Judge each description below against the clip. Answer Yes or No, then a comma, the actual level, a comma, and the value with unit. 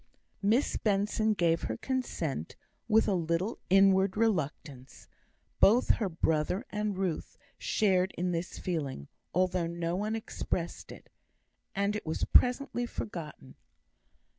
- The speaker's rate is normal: No, slow, 120 wpm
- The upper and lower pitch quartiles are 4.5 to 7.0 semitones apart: No, average, 4.1 semitones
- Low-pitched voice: No, medium, 185 Hz